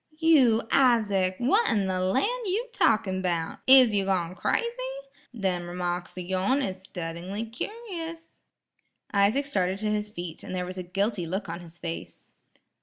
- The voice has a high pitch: Yes, high, 195 Hz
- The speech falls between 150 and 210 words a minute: Yes, average, 160 wpm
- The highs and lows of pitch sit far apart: Yes, wide, 6.1 semitones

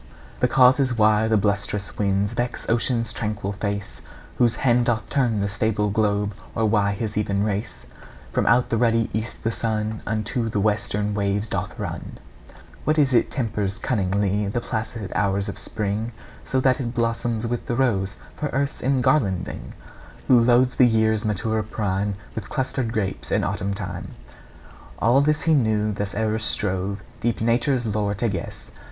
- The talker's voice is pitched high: No, low, 110 Hz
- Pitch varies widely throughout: No, average, 2.7 semitones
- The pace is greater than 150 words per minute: Yes, average, 165 wpm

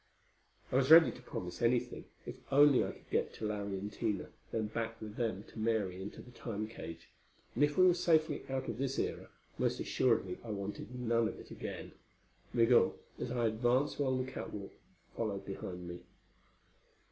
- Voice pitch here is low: Yes, low, 115 Hz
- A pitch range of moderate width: Yes, average, 3.9 semitones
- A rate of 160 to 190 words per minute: Yes, average, 180 wpm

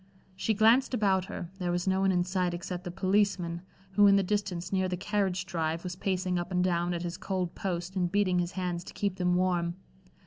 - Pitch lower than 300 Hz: Yes, medium, 185 Hz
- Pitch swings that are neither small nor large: No, narrow, 1.7 semitones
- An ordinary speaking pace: No, fast, 220 wpm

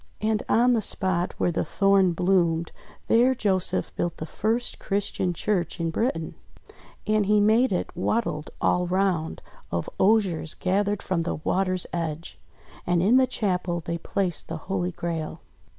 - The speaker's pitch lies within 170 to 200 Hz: Yes, medium, 185 Hz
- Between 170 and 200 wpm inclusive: No, average, 150 wpm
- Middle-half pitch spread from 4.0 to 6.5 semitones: No, average, 3.6 semitones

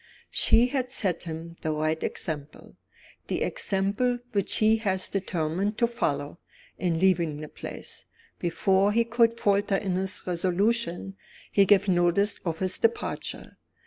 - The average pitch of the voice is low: No, high, 190 Hz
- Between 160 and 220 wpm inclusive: No, average, 140 wpm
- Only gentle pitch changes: No, average, 3.9 semitones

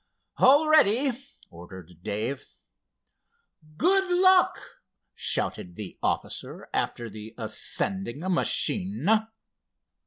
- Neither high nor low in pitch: Yes, medium, 170 Hz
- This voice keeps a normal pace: No, slow, 75 wpm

